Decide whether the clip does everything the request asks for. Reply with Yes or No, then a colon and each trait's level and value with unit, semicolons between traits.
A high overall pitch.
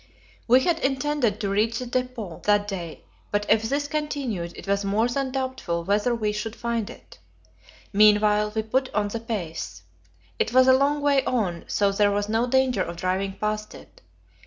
Yes: high, 220 Hz